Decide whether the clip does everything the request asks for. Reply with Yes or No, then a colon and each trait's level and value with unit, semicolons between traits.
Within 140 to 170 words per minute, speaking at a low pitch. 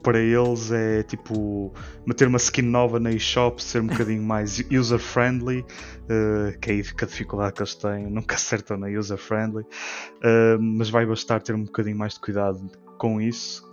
No: fast, 185 wpm; low, 110 Hz